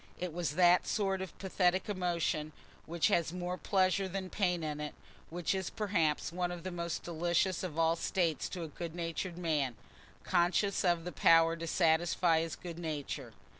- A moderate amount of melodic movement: No, narrow, 2.0 semitones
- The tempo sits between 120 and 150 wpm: No, average, 170 wpm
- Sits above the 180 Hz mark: No, medium, 175 Hz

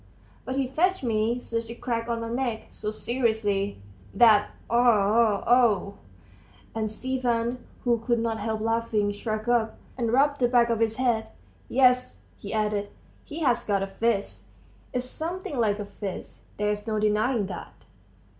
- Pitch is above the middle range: Yes, high, 230 Hz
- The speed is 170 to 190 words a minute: No, average, 155 wpm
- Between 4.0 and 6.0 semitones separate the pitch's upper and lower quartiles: No, narrow, 2.6 semitones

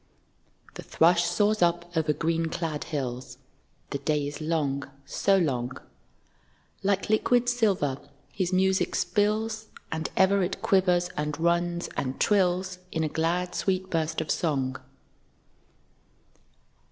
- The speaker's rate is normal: No, slow, 125 wpm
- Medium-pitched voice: Yes, medium, 170 Hz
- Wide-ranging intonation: No, average, 4.0 semitones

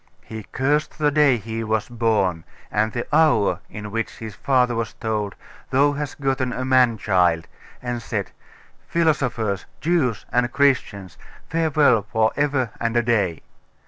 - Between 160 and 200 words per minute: No, average, 145 wpm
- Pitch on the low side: Yes, low, 120 Hz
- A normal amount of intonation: Yes, average, 4.2 semitones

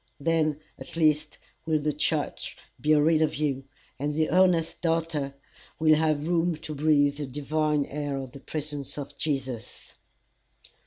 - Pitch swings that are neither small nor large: No, narrow, 1.7 semitones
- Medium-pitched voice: Yes, medium, 150 Hz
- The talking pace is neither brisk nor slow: Yes, average, 150 wpm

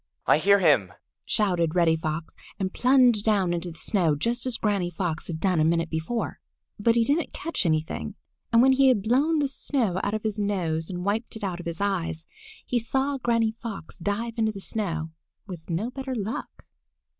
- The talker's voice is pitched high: Yes, high, 200 Hz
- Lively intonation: Yes, wide, 5.7 semitones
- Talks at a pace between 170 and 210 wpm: Yes, average, 195 wpm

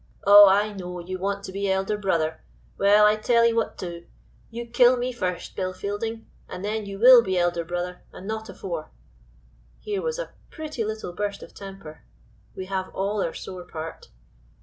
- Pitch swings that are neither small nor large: Yes, average, 3.3 semitones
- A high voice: Yes, high, 200 Hz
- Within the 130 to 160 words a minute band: No, average, 180 wpm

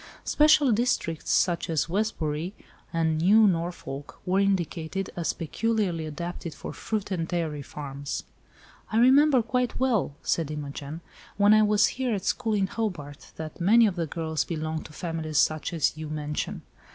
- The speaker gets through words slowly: No, average, 155 wpm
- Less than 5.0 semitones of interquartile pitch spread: No, average, 5.3 semitones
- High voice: No, medium, 170 Hz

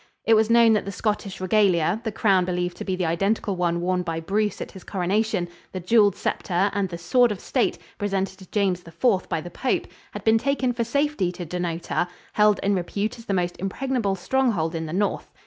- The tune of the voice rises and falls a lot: No, average, 3.6 semitones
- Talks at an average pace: No, fast, 210 wpm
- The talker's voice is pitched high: Yes, high, 195 Hz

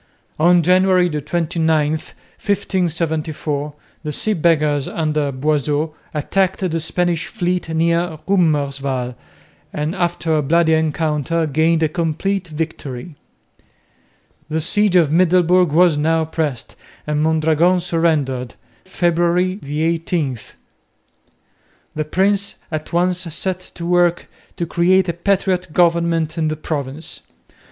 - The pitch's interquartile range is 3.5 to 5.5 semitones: No, narrow, 2.6 semitones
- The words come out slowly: Yes, slow, 110 wpm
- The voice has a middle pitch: Yes, medium, 165 Hz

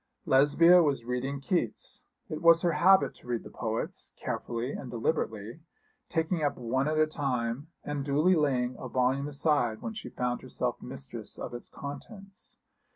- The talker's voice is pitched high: No, medium, 140 Hz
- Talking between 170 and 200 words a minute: No, average, 160 wpm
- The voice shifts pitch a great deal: No, average, 4.5 semitones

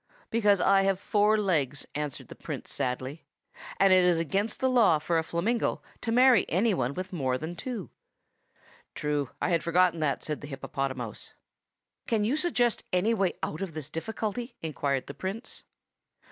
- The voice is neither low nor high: Yes, medium, 180 Hz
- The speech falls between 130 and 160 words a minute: No, average, 170 wpm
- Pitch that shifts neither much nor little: No, wide, 6.2 semitones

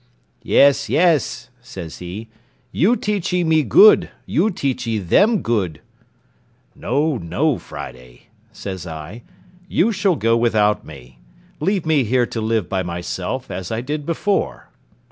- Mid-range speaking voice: No, low, 120 Hz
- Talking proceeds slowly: Yes, slow, 130 wpm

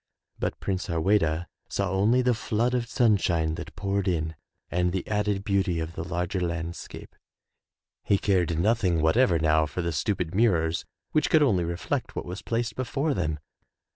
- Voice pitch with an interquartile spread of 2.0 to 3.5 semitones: No, average, 4.2 semitones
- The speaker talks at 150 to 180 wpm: Yes, average, 170 wpm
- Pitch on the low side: Yes, very low, 95 Hz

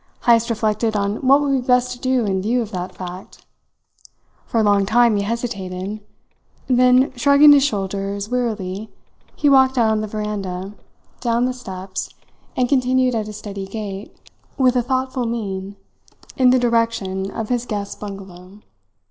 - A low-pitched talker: No, high, 220 Hz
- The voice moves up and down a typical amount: Yes, average, 4.0 semitones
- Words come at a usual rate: Yes, average, 160 wpm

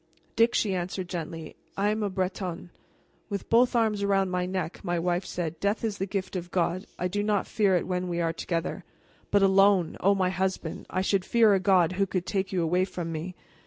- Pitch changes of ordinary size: No, narrow, 2.1 semitones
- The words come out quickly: Yes, fast, 215 wpm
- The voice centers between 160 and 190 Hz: Yes, medium, 185 Hz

